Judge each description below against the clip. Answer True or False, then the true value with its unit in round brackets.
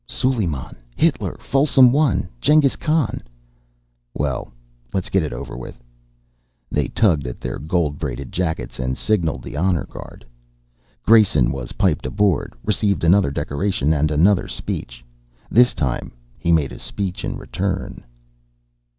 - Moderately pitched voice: False (85 Hz)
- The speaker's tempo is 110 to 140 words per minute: True (135 wpm)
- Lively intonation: True (6.9 semitones)